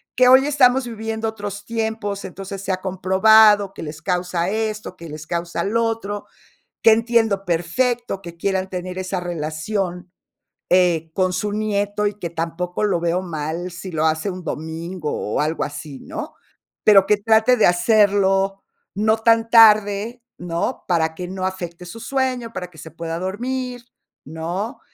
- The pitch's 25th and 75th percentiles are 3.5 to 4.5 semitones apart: Yes, average, 4.1 semitones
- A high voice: Yes, high, 195 Hz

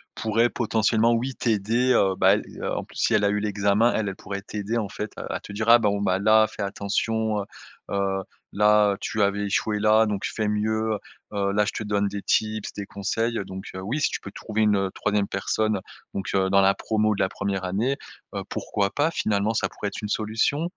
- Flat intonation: Yes, narrow, 1.7 semitones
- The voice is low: Yes, low, 105 Hz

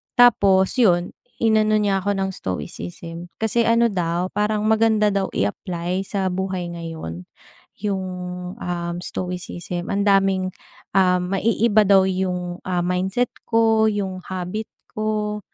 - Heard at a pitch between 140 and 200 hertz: Yes, high, 190 Hz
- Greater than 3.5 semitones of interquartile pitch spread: No, average, 3.0 semitones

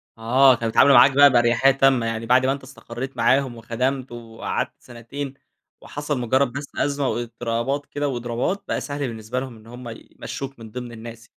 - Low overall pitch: Yes, low, 125 Hz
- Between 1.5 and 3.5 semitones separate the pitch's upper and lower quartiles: Yes, average, 2.7 semitones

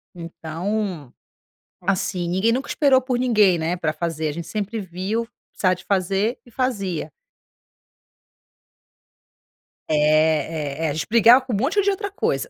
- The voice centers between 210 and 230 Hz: No, high, 190 Hz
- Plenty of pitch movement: Yes, wide, 6.0 semitones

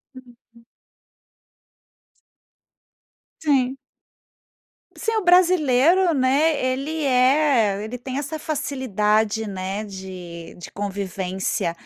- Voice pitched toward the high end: Yes, very high, 255 Hz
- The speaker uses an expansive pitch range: Yes, wide, 6.6 semitones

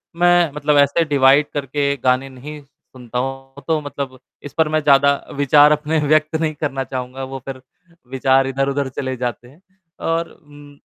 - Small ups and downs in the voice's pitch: Yes, narrow, 2.0 semitones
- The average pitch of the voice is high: No, medium, 140 Hz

